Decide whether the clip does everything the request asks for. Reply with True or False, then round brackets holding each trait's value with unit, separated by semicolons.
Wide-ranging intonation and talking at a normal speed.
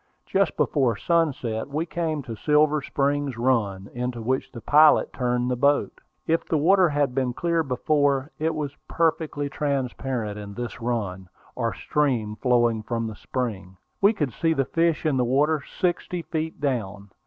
False (4.5 semitones; 165 wpm)